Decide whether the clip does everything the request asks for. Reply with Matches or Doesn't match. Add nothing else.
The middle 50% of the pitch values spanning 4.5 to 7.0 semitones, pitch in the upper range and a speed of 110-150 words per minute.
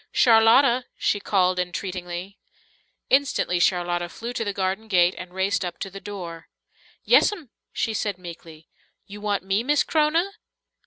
Doesn't match